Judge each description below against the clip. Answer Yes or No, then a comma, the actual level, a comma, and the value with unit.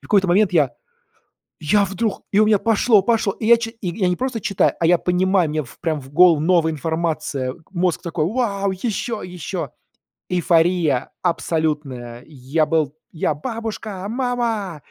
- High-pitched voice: No, medium, 180 Hz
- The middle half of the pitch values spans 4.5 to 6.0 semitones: Yes, average, 4.9 semitones